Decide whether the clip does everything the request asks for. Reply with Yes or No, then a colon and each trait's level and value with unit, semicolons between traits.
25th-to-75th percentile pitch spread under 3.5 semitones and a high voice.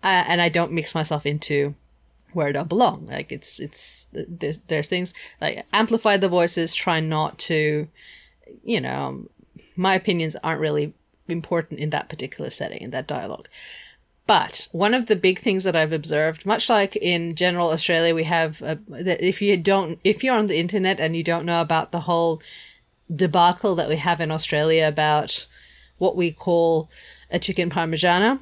No: average, 2.7 semitones; medium, 170 Hz